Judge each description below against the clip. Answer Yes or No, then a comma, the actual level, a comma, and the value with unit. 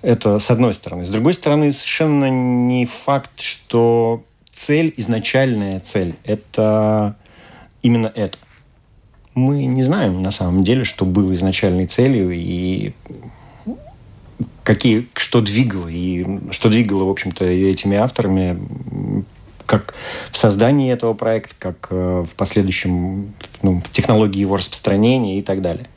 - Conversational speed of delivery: Yes, average, 120 wpm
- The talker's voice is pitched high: No, low, 105 Hz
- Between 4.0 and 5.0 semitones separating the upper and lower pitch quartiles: Yes, average, 4.3 semitones